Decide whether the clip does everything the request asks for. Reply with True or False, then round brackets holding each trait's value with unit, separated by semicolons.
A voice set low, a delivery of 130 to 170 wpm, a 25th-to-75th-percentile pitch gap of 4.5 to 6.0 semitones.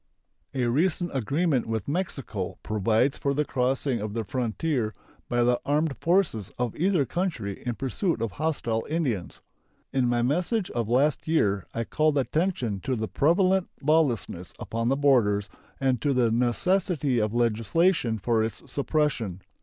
True (130 Hz; 150 wpm; 5.4 semitones)